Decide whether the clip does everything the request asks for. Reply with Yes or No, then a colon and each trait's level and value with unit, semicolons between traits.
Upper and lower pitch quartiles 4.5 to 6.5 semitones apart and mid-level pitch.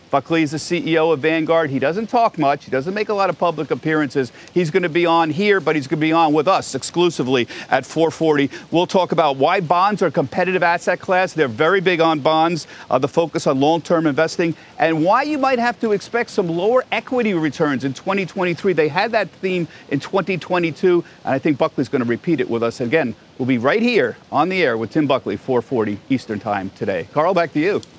No: average, 3.5 semitones; medium, 165 Hz